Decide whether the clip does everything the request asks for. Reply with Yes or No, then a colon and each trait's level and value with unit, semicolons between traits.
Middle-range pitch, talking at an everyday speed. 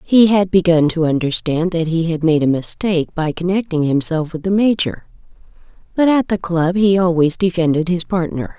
Yes: medium, 170 Hz; average, 180 wpm